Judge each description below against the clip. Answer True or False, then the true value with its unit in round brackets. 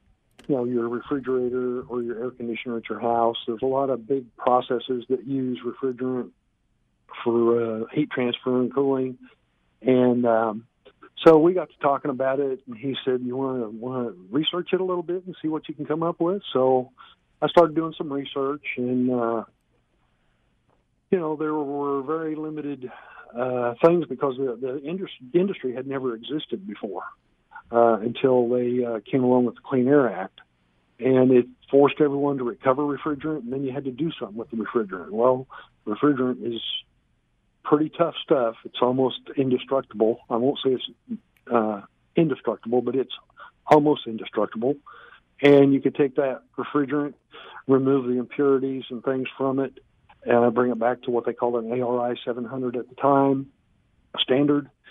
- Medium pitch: False (130 Hz)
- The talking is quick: False (170 wpm)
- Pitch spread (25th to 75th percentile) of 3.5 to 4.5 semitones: False (2.9 semitones)